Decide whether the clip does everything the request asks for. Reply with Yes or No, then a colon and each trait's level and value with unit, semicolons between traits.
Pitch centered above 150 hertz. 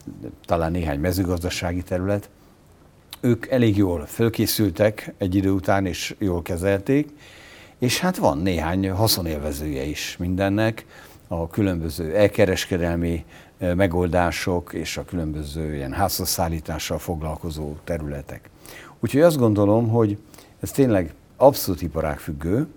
No: very low, 90 Hz